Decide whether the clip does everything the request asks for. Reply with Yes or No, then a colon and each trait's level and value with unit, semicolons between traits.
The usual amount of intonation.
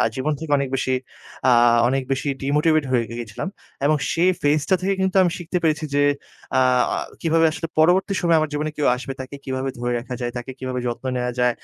Yes: average, 3.9 semitones